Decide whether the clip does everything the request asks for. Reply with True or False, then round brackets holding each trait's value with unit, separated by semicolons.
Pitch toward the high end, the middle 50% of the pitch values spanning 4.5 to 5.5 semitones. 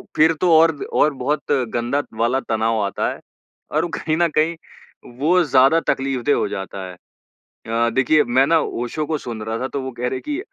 False (135 Hz; 4.9 semitones)